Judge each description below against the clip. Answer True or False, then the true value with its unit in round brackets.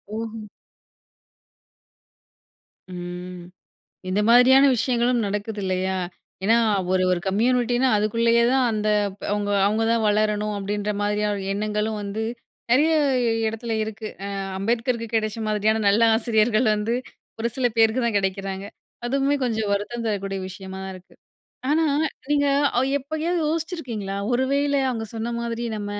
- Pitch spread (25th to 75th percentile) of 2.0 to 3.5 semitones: True (2.9 semitones)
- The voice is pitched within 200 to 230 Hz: True (220 Hz)